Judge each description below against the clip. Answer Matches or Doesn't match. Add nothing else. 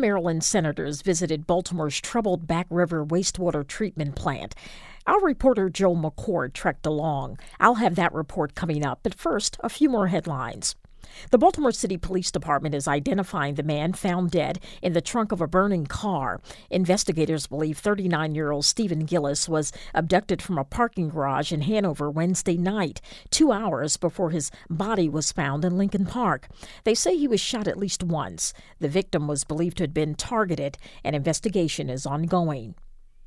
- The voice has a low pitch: Doesn't match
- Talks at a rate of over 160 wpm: Matches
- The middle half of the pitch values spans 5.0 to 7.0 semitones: Doesn't match